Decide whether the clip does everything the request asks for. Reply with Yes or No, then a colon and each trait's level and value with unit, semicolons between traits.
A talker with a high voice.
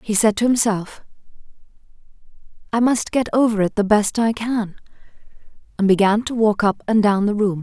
Yes: high, 215 Hz